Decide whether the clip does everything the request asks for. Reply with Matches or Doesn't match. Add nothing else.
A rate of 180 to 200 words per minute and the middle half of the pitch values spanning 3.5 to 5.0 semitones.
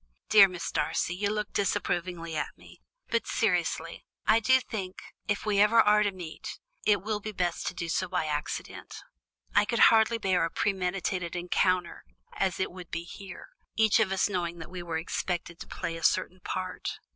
Doesn't match